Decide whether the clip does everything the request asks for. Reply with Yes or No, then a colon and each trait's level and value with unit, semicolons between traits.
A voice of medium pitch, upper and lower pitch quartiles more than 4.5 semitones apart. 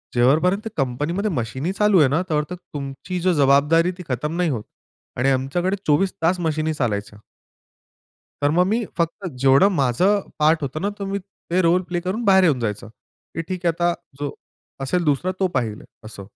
Yes: medium, 160 Hz; average, 5.1 semitones